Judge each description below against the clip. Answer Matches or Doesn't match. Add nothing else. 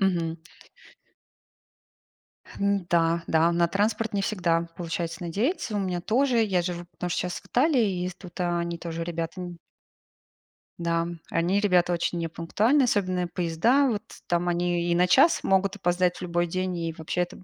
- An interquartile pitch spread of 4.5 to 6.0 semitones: Doesn't match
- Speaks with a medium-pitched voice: Matches